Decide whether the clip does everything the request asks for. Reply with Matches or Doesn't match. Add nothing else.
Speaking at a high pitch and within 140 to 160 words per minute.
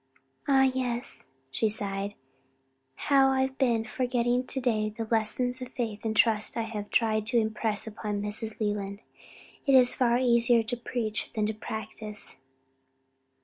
Matches